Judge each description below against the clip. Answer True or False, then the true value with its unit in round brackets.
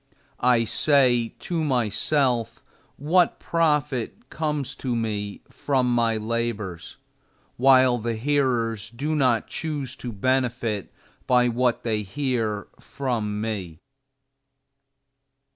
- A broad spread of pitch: False (3.3 semitones)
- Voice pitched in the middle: False (120 Hz)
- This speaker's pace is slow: True (100 wpm)